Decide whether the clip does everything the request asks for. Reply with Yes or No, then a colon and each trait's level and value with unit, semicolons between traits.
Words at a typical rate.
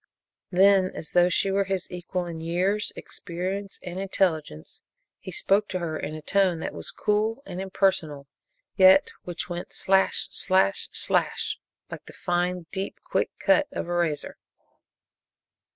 Yes: average, 150 wpm